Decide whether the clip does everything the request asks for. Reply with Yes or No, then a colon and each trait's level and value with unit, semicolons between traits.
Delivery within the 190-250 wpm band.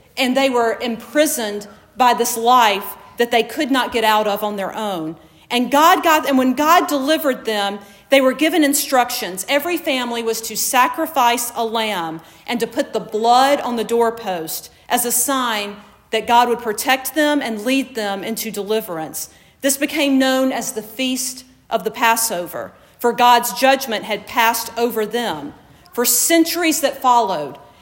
No: average, 165 wpm